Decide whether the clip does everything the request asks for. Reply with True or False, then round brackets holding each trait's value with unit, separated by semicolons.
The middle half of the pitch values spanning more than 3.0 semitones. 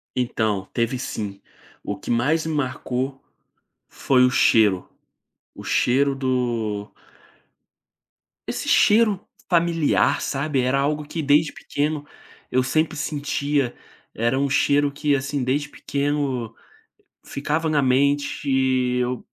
False (2.7 semitones)